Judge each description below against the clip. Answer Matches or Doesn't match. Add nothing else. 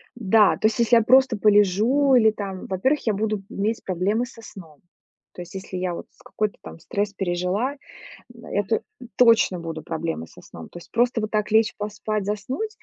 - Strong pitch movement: Doesn't match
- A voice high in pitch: Matches